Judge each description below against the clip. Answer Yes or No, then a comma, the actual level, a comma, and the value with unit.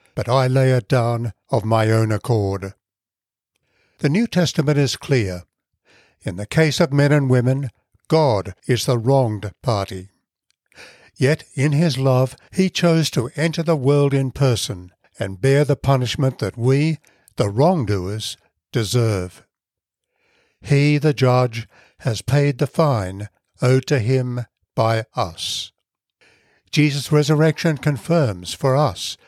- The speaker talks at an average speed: No, slow, 130 wpm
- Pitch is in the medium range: No, low, 130 Hz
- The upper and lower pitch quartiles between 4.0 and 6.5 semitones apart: Yes, average, 4.6 semitones